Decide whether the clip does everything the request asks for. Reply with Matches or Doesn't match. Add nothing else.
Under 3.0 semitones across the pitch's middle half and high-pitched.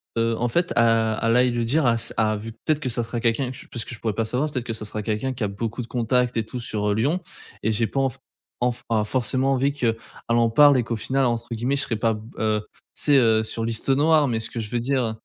Doesn't match